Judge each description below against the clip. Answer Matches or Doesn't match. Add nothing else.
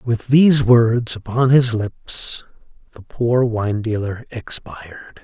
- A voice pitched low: Matches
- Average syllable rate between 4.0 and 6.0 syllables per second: Doesn't match